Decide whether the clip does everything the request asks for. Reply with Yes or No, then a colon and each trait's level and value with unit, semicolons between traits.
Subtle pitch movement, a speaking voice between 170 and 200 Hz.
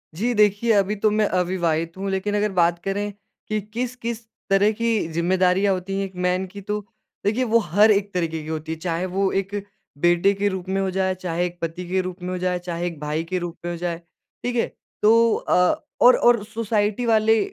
No: average, 3.0 semitones; high, 190 Hz